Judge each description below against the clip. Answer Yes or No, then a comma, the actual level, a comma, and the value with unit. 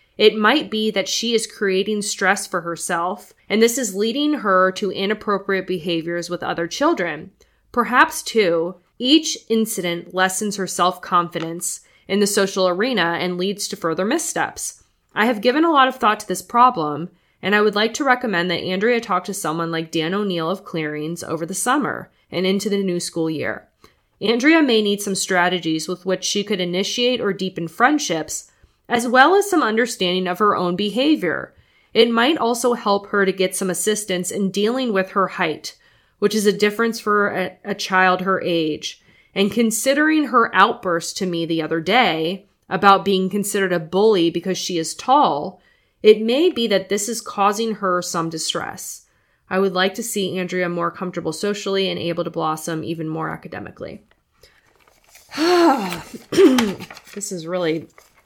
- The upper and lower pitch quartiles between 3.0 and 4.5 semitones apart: Yes, average, 3.8 semitones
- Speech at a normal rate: Yes, average, 170 wpm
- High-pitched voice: Yes, high, 195 Hz